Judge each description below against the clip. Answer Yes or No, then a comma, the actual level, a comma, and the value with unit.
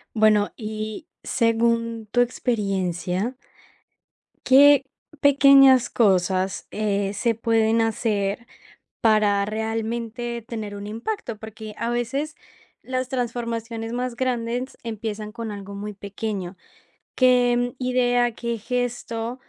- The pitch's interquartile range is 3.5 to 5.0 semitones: No, narrow, 2.5 semitones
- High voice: Yes, high, 230 Hz